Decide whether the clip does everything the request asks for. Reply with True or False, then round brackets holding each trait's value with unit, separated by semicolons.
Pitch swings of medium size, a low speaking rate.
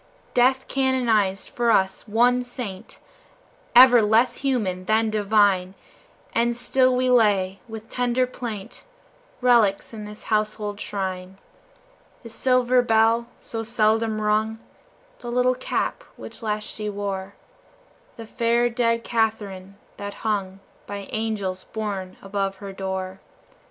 True (3.2 semitones; 120 wpm)